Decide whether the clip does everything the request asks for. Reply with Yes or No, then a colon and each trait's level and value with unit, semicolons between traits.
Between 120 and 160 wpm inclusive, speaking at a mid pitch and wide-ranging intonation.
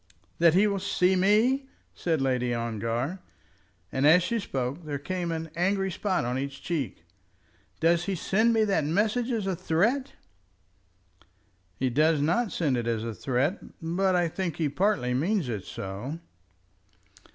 Yes: average, 155 wpm; medium, 165 Hz; wide, 6.4 semitones